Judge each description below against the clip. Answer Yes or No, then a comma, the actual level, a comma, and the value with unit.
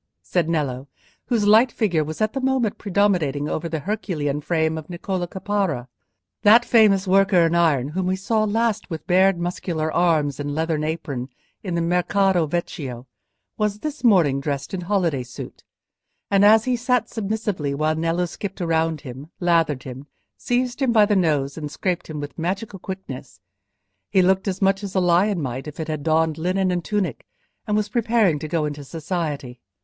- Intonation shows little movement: No, average, 4.8 semitones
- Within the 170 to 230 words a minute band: Yes, average, 175 wpm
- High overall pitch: No, medium, 175 Hz